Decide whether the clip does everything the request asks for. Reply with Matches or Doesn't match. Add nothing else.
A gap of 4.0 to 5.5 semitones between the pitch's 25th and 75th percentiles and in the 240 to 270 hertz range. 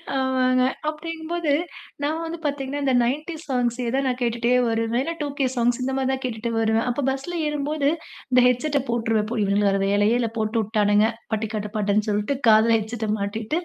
Matches